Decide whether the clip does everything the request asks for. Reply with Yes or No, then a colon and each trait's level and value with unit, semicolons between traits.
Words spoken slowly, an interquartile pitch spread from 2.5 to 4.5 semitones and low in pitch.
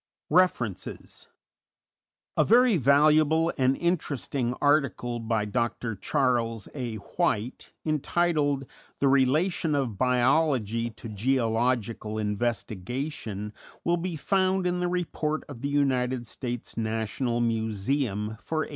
No: slow, 110 wpm; average, 5.2 semitones; low, 130 Hz